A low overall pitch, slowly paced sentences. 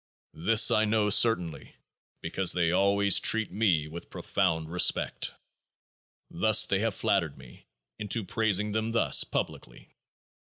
Yes: low, 100 Hz; slow, 125 wpm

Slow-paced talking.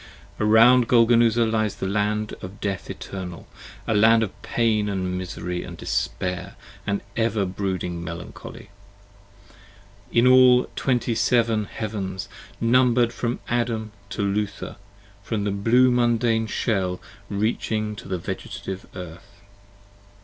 Yes: slow, 125 wpm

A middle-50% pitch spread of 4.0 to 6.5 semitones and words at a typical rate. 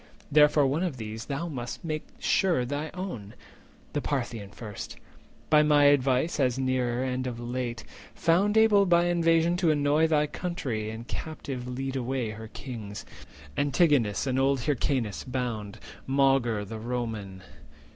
Yes: average, 4.3 semitones; average, 145 wpm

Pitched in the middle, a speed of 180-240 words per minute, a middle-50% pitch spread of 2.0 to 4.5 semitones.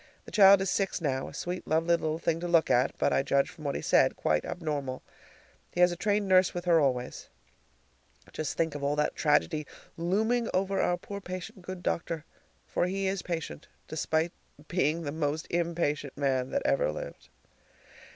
Yes: medium, 170 Hz; average, 185 wpm; average, 3.8 semitones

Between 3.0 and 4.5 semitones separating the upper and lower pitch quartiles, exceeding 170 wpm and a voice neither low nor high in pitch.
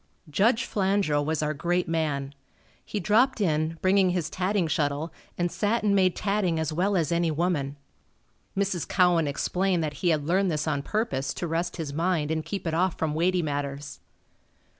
Yes: average, 3.7 semitones; average, 180 wpm; medium, 170 Hz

